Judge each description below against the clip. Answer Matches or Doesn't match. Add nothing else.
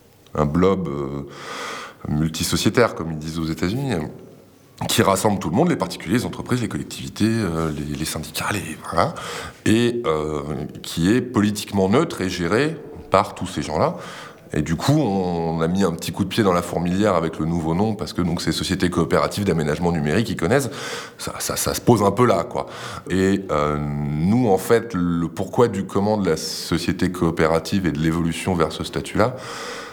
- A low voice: Matches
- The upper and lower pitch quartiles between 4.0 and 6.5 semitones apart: Doesn't match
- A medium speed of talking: Matches